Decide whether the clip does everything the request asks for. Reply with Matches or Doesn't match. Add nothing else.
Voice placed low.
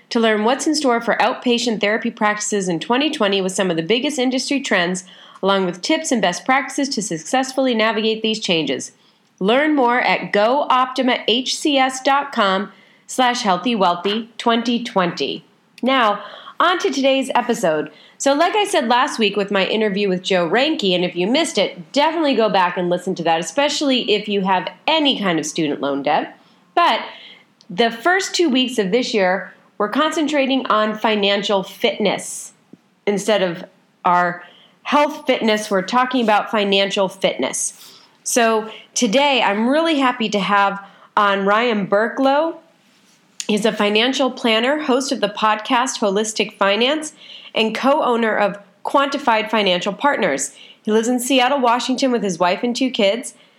Doesn't match